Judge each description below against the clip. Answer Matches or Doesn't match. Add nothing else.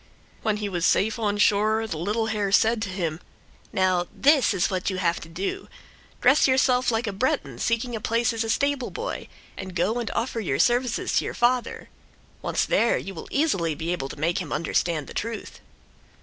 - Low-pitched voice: Doesn't match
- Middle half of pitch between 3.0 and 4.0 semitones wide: Doesn't match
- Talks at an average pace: Matches